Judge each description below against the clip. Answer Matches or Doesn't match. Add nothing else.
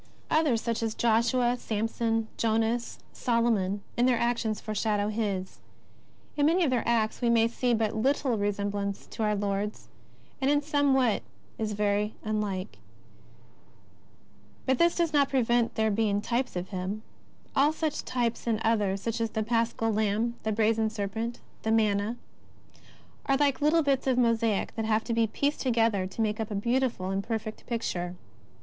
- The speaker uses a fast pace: Doesn't match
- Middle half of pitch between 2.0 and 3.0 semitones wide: Matches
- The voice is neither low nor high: Doesn't match